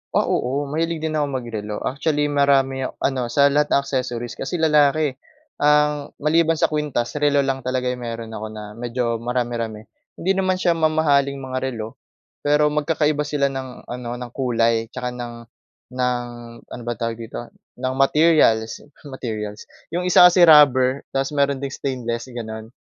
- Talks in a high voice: No, low, 135 Hz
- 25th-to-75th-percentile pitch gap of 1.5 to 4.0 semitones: Yes, average, 3.7 semitones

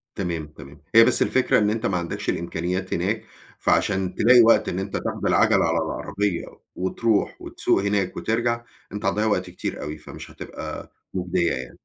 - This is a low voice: Yes, very low, 95 Hz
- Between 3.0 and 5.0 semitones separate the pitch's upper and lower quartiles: Yes, average, 4.0 semitones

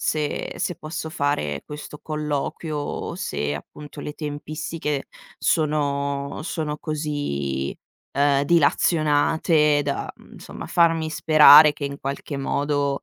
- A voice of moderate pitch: Yes, medium, 150 Hz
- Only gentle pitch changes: Yes, narrow, 1.6 semitones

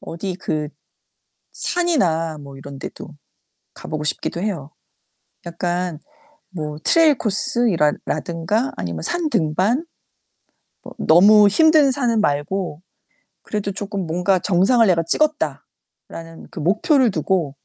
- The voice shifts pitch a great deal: Yes, wide, 6.0 semitones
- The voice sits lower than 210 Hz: Yes, medium, 185 Hz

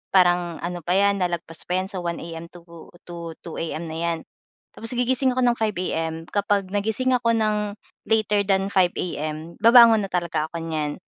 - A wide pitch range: No, average, 4.1 semitones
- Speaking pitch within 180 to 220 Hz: Yes, medium, 185 Hz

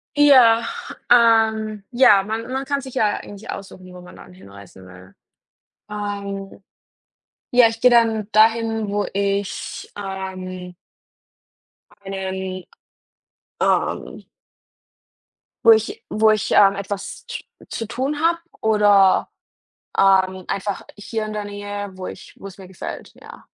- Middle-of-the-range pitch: No, high, 205 Hz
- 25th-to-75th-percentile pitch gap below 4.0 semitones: Yes, average, 2.9 semitones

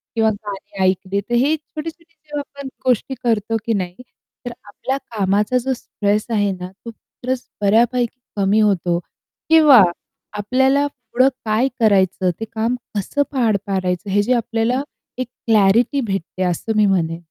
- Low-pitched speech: No, high, 220 Hz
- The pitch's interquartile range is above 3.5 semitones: Yes, average, 4.3 semitones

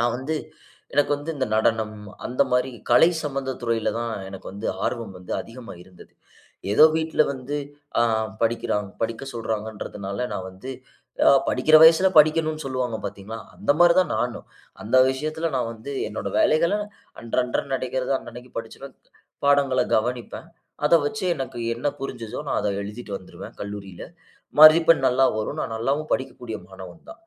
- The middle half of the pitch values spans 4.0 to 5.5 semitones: Yes, average, 4.4 semitones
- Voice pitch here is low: Yes, low, 125 Hz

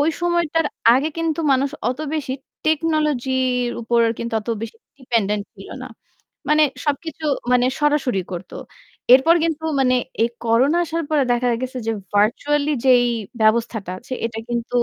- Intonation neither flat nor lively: Yes, average, 4.5 semitones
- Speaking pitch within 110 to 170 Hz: No, very high, 260 Hz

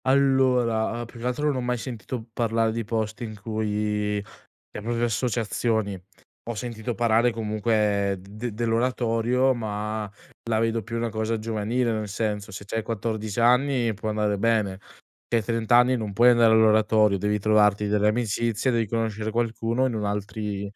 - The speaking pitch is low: Yes, low, 110 Hz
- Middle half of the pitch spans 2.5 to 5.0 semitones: No, narrow, 1.9 semitones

